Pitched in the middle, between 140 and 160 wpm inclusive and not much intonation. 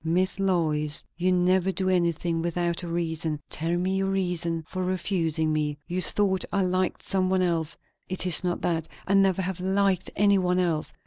No: medium, 180 Hz; average, 185 wpm; narrow, 2.2 semitones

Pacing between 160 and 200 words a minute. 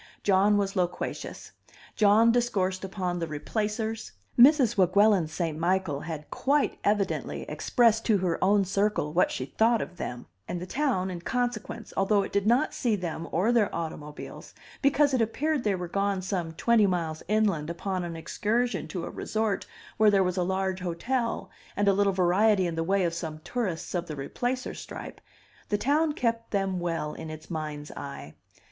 Yes: average, 175 wpm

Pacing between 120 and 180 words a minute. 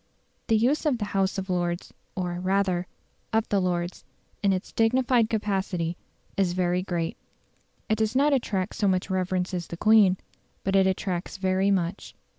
Yes: average, 165 wpm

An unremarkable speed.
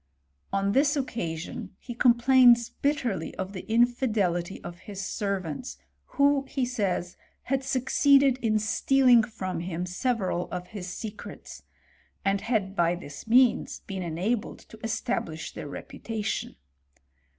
No: slow, 125 wpm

